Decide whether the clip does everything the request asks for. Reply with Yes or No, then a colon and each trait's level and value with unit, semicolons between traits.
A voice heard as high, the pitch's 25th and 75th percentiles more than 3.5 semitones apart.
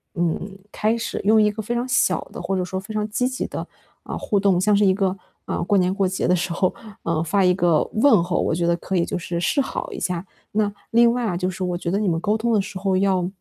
No: high, 195 Hz; average, 3.1 semitones